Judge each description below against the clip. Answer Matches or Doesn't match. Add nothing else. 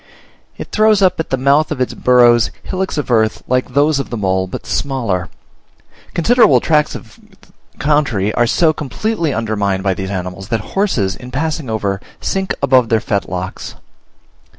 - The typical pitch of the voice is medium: Doesn't match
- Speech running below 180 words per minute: Matches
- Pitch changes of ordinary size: Doesn't match